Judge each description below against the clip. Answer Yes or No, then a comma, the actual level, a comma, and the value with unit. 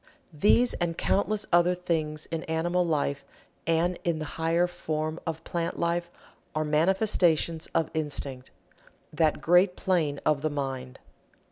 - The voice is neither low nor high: Yes, medium, 165 Hz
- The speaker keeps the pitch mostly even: Yes, narrow, 2.3 semitones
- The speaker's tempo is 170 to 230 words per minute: No, slow, 135 wpm